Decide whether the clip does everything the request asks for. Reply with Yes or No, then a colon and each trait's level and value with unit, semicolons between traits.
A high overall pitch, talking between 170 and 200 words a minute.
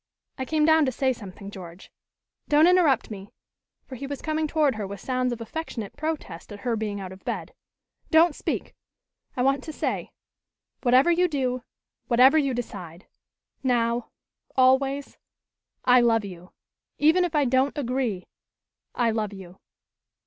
No: very high, 255 Hz; average, 155 wpm